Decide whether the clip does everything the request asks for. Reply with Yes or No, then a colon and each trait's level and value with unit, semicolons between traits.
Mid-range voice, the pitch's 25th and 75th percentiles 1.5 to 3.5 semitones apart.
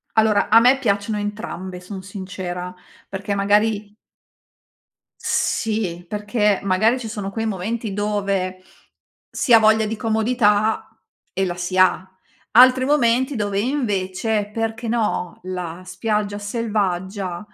No: high, 205 Hz; average, 2.8 semitones